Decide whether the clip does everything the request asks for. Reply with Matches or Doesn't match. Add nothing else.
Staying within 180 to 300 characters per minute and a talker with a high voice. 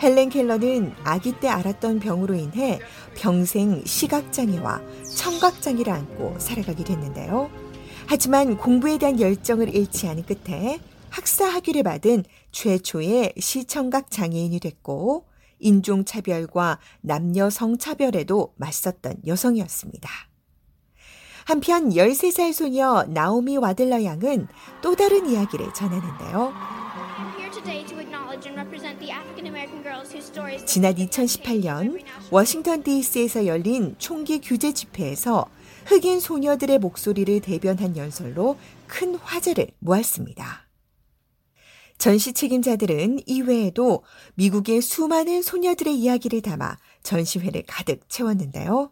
Matches